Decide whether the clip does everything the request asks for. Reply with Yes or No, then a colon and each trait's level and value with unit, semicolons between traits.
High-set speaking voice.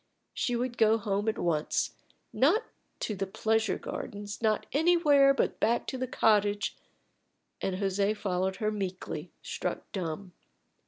Yes: high, 210 Hz